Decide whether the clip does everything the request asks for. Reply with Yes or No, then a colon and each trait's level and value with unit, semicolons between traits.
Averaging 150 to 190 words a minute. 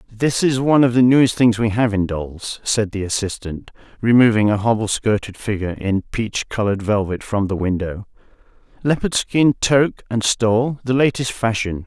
Yes: average, 170 wpm